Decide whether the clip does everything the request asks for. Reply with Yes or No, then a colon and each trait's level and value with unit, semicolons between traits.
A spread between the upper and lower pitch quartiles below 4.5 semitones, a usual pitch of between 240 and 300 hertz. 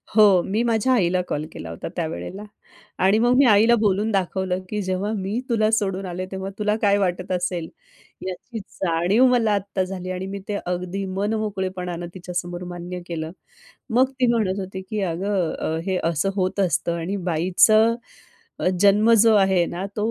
No: average, 2.8 semitones; high, 190 Hz